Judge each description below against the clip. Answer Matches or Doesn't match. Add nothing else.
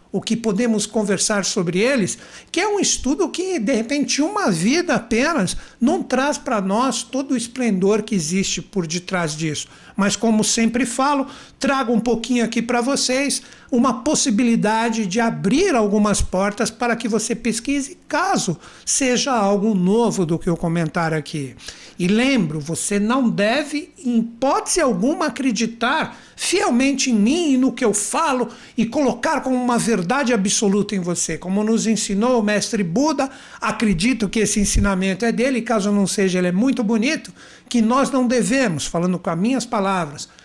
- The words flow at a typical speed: Matches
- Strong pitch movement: Doesn't match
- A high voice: Matches